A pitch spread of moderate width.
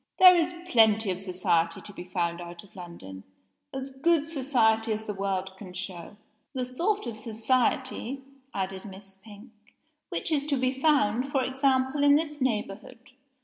No: wide, 5.7 semitones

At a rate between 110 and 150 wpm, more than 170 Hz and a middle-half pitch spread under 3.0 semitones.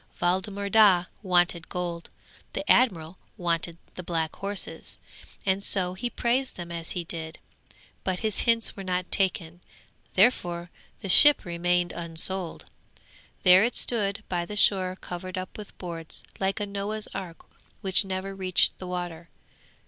Yes: average, 145 wpm; medium, 185 Hz; narrow, 2.4 semitones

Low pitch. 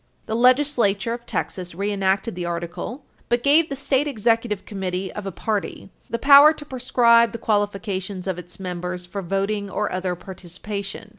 No: high, 205 Hz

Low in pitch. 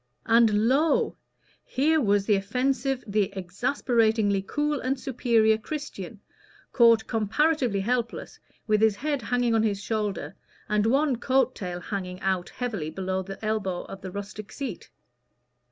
No: high, 220 Hz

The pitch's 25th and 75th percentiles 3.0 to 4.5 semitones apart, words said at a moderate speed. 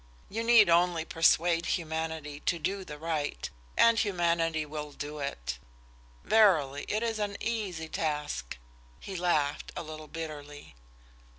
No: average, 3.8 semitones; slow, 125 wpm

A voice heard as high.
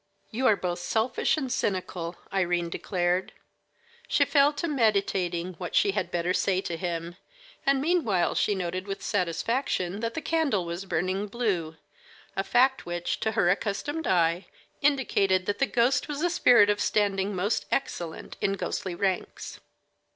Yes: high, 195 Hz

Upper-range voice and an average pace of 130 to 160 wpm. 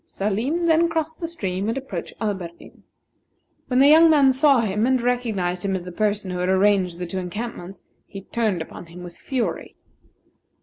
No: high, 210 Hz; average, 180 wpm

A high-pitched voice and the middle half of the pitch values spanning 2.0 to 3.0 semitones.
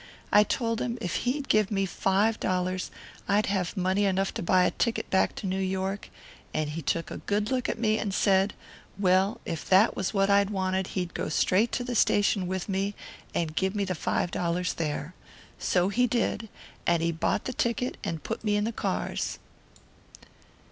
Yes: high, 195 Hz; narrow, 2.6 semitones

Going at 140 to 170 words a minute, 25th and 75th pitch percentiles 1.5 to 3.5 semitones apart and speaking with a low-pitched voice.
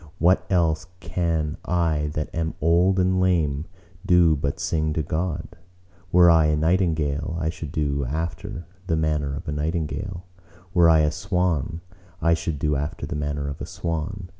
Yes: average, 165 wpm; narrow, 2.6 semitones; very low, 80 Hz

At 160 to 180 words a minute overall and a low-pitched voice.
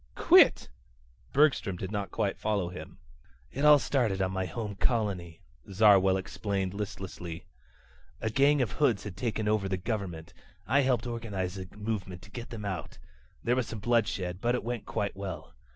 Yes: average, 165 wpm; low, 105 Hz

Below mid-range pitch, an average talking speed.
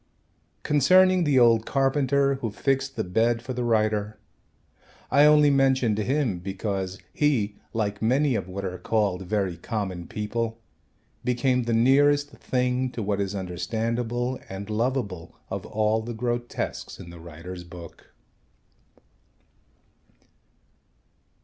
No: low, 115 Hz; slow, 125 wpm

